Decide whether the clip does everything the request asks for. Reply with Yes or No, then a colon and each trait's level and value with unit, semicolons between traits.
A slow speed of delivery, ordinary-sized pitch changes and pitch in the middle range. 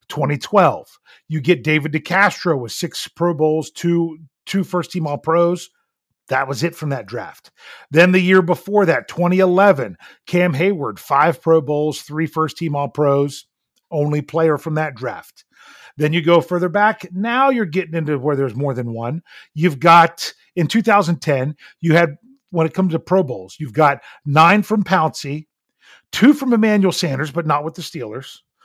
No: average, 170 wpm; average, 3.4 semitones; medium, 165 Hz